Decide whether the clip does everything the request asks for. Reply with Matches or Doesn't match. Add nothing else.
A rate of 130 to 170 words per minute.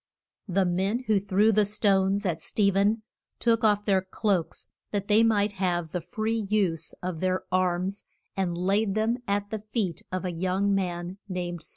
Doesn't match